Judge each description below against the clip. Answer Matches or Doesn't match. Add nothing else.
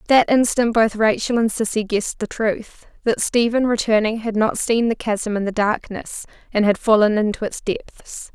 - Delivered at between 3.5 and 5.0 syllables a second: Matches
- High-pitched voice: Matches